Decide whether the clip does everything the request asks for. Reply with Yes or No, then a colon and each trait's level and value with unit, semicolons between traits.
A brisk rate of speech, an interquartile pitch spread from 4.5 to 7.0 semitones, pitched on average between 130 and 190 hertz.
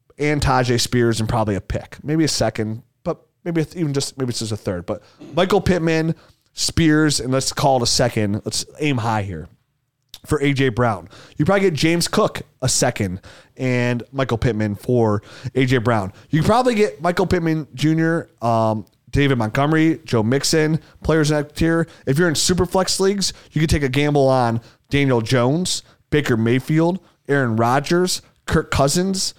No: average, 170 wpm; average, 5.2 semitones; low, 135 Hz